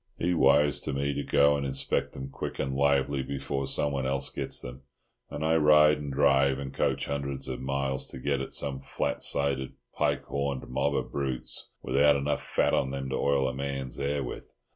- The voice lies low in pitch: Yes, very low, 70 Hz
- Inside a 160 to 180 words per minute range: No, average, 200 wpm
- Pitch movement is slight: Yes, narrow, 1.1 semitones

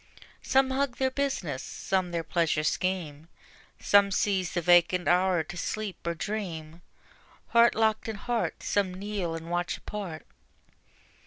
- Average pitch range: Yes, average, 4.0 semitones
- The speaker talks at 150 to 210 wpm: No, average, 140 wpm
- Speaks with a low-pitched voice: No, medium, 185 Hz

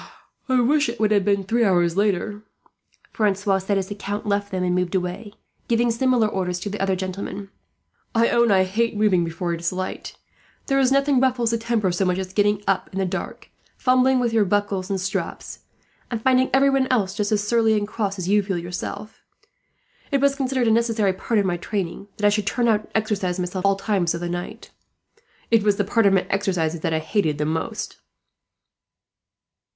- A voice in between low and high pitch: No, high, 205 Hz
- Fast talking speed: Yes, fast, 210 wpm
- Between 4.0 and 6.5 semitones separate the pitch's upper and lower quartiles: No, average, 3.6 semitones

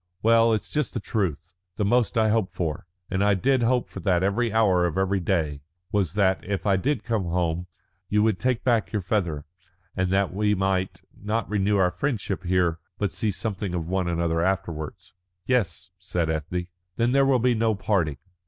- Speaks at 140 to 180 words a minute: No, average, 190 wpm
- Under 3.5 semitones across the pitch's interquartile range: No, average, 3.9 semitones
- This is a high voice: No, very low, 95 Hz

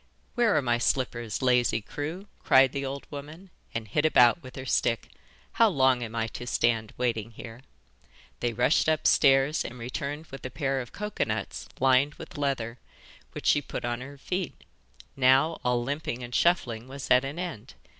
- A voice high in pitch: No, low, 130 Hz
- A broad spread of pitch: No, average, 3.3 semitones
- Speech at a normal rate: Yes, average, 180 wpm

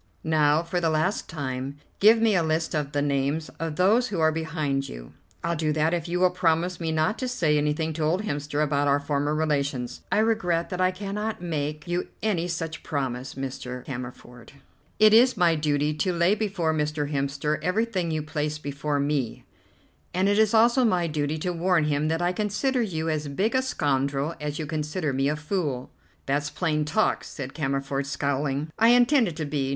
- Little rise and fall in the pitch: No, average, 3.9 semitones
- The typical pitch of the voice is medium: Yes, medium, 155 Hz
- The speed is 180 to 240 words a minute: Yes, average, 195 wpm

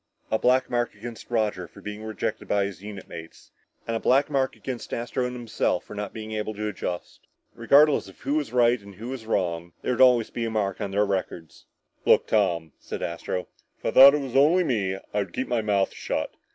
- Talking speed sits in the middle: No, fast, 220 wpm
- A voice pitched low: Yes, low, 110 Hz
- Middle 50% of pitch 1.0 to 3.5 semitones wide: No, average, 4.0 semitones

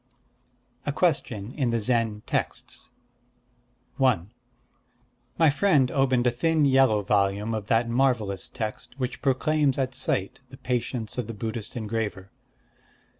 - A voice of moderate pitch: No, low, 120 Hz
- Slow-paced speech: Yes, slow, 130 wpm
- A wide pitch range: No, average, 3.7 semitones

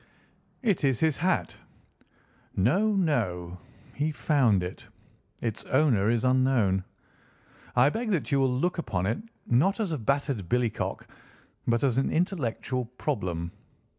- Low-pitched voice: Yes, low, 130 Hz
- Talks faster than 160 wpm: No, slow, 135 wpm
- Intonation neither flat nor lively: No, wide, 5.9 semitones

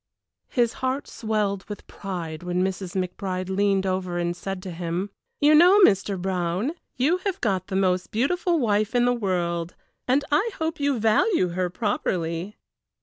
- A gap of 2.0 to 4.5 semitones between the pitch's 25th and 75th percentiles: No, average, 5.3 semitones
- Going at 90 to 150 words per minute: No, average, 160 wpm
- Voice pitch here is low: No, high, 195 Hz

